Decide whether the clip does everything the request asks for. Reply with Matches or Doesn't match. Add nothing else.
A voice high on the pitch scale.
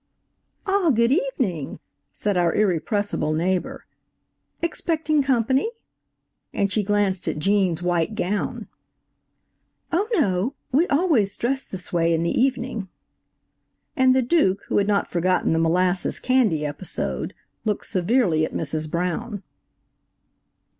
Matches